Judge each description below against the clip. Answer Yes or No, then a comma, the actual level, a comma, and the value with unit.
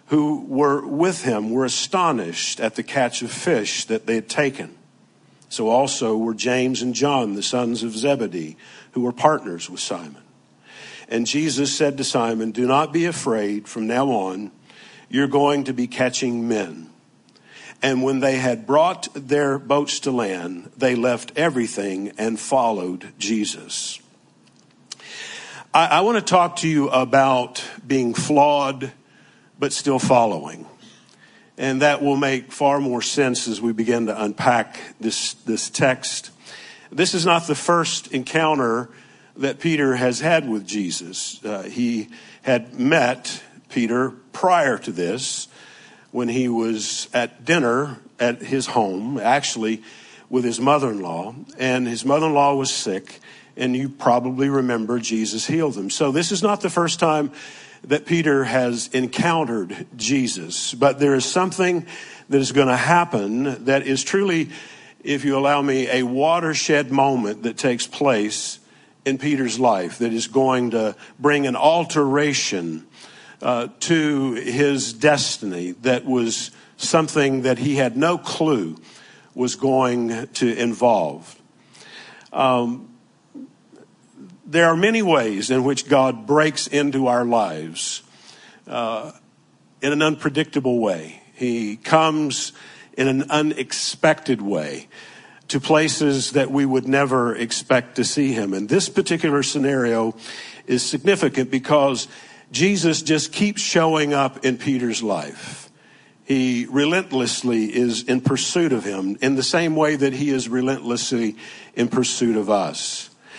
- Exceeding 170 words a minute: No, average, 140 wpm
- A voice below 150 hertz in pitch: Yes, low, 135 Hz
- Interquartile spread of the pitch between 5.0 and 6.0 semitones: No, average, 3.5 semitones